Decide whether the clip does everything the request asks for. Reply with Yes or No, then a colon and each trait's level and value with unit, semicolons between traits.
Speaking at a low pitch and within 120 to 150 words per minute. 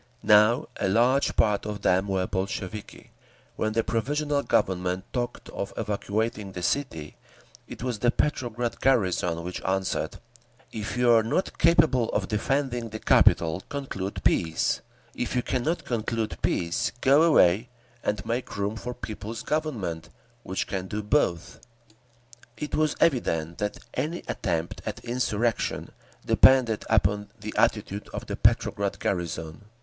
Yes: low, 110 Hz; average, 140 wpm